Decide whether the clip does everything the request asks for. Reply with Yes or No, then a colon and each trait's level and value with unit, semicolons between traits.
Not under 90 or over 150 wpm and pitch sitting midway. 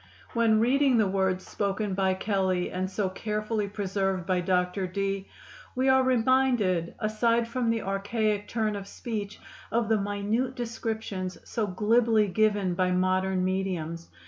No: average, 145 wpm; high, 205 Hz